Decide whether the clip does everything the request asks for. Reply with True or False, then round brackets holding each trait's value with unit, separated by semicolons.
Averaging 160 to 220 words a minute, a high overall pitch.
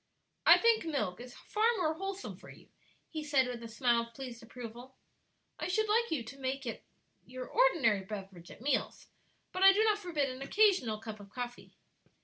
True (190 wpm; 265 Hz)